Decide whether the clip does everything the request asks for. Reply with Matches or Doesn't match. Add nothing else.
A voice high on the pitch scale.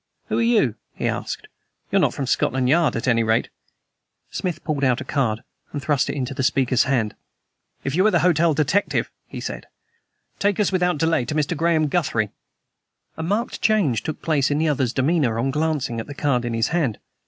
Doesn't match